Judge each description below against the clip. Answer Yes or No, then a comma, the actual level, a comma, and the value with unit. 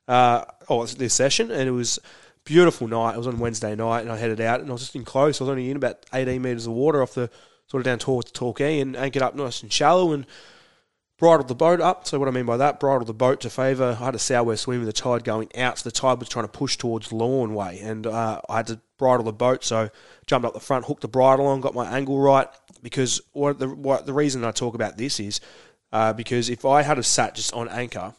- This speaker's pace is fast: Yes, fast, 275 wpm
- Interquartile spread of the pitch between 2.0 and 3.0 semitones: Yes, average, 2.7 semitones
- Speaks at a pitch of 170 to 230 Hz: No, low, 125 Hz